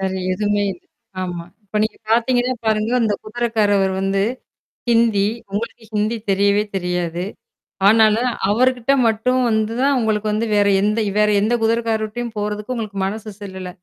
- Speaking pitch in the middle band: No, high, 215 Hz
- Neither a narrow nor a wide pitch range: No, narrow, 2.2 semitones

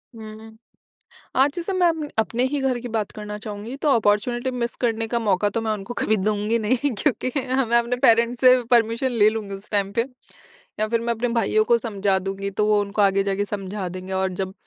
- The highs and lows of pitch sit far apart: No, average, 2.9 semitones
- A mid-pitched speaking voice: No, high, 220 Hz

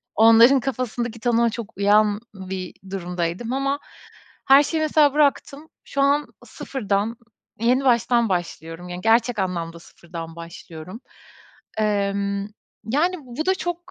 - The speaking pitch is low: No, high, 225 Hz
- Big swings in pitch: Yes, wide, 6.1 semitones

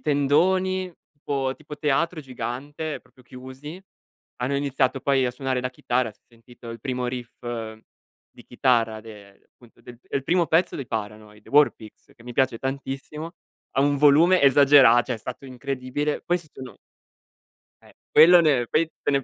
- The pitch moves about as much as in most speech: Yes, average, 3.2 semitones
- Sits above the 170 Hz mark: No, low, 135 Hz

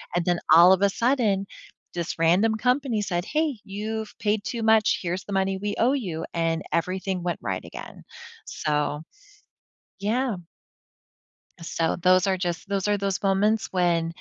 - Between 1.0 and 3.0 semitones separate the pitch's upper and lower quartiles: No, average, 3.8 semitones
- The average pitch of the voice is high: Yes, high, 195 Hz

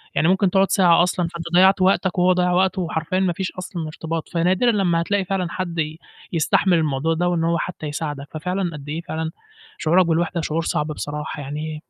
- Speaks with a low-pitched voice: No, medium, 170 Hz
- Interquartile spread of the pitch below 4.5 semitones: Yes, narrow, 2.6 semitones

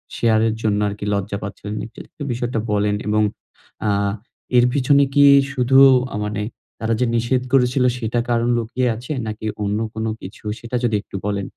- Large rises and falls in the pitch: No, average, 2.9 semitones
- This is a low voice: Yes, low, 115 Hz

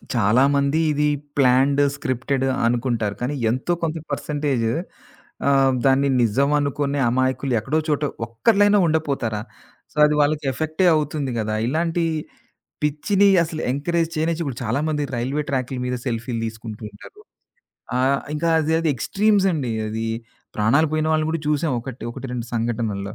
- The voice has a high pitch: No, medium, 140 Hz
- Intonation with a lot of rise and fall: No, average, 4.2 semitones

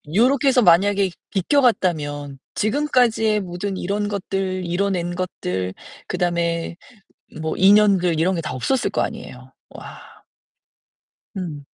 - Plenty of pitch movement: No, average, 3.5 semitones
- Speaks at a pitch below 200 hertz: Yes, medium, 185 Hz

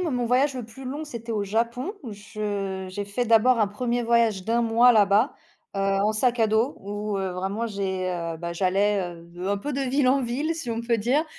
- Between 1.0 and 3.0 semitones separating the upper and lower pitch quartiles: No, average, 3.6 semitones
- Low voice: No, high, 225 Hz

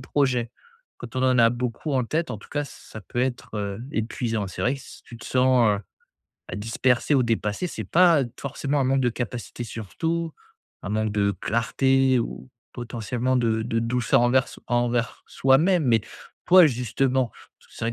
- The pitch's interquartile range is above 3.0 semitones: No, average, 2.7 semitones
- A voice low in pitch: Yes, low, 125 Hz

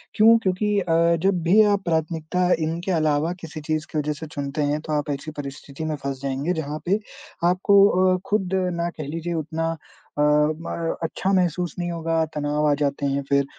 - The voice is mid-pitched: Yes, medium, 160 Hz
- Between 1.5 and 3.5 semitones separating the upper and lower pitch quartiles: Yes, average, 2.9 semitones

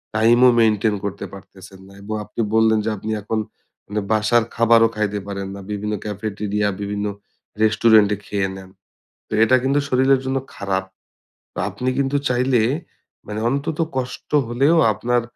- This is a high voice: No, low, 110 Hz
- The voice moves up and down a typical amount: Yes, average, 3.1 semitones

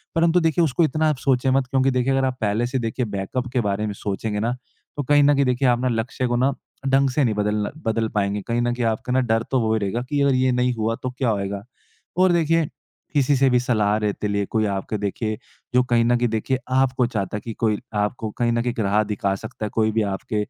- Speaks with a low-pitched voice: Yes, low, 120 Hz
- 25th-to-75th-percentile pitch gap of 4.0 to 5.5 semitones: No, average, 3.6 semitones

